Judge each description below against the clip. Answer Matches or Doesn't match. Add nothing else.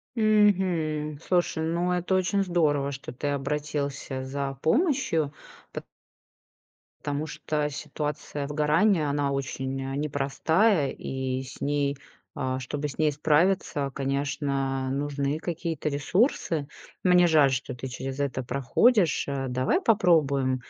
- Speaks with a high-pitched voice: Doesn't match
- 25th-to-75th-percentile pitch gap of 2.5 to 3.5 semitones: Matches